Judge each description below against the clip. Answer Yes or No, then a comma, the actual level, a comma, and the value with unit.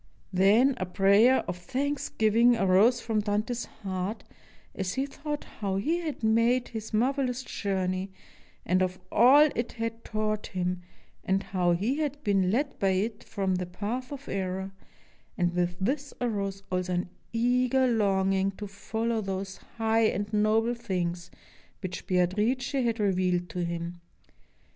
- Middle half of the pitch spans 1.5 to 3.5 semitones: No, average, 4.3 semitones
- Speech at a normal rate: Yes, average, 150 wpm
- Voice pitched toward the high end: Yes, high, 210 Hz